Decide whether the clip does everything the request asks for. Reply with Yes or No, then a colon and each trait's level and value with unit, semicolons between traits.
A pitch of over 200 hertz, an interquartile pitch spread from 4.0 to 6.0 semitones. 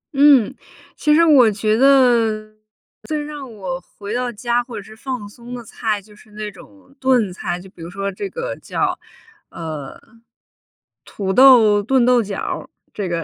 Yes: high, 220 Hz; average, 4.3 semitones